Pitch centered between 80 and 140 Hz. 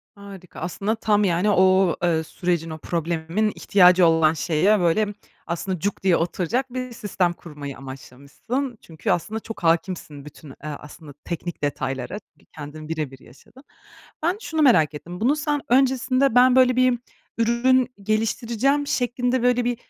No: high, 190 Hz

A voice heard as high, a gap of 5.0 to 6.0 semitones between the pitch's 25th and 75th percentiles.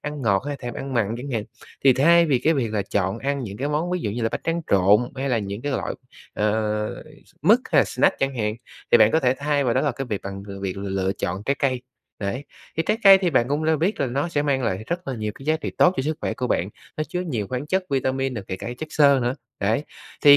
No: low, 130 Hz; wide, 5.6 semitones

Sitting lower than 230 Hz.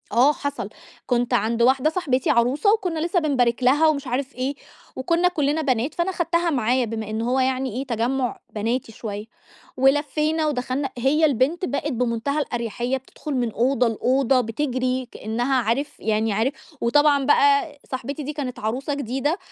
No: very high, 265 Hz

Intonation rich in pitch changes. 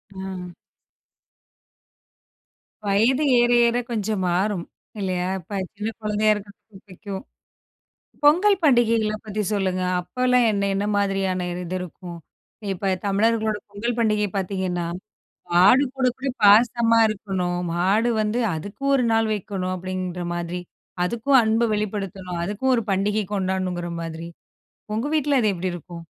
No: average, 3.4 semitones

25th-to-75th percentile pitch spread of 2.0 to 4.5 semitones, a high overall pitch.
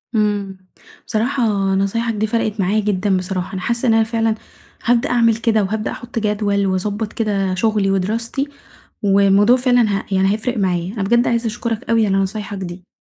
Yes: average, 2.8 semitones; high, 210 Hz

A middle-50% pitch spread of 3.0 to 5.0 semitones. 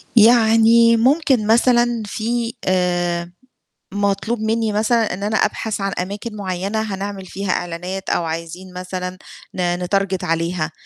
Yes: average, 3.7 semitones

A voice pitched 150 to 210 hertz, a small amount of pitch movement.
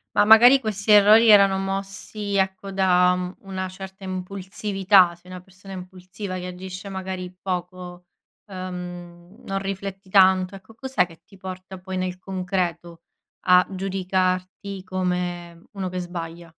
Yes: medium, 185 Hz; narrow, 1.3 semitones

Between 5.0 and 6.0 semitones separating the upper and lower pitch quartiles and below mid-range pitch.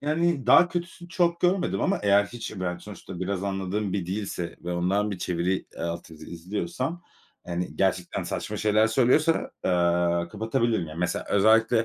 Yes: wide, 5.4 semitones; low, 100 Hz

